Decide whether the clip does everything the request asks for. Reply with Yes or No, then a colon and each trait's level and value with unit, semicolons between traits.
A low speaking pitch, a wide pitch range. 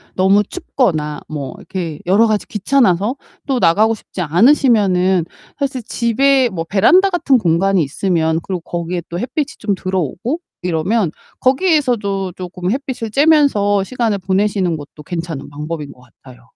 No: high, 195 Hz; wide, 6.0 semitones